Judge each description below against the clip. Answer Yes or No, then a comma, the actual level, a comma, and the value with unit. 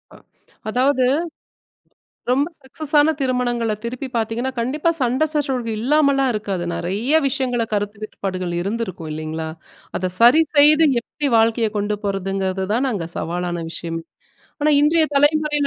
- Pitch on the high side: Yes, high, 235 Hz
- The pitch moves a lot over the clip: Yes, wide, 6.2 semitones